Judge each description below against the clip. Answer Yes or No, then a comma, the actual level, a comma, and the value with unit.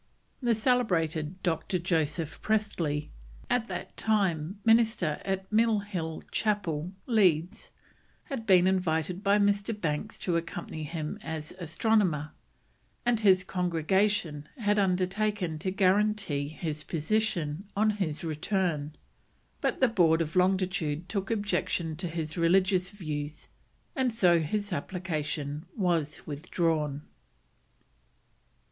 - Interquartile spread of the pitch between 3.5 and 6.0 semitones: Yes, average, 4.5 semitones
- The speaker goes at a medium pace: No, slow, 115 wpm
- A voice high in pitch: No, medium, 180 Hz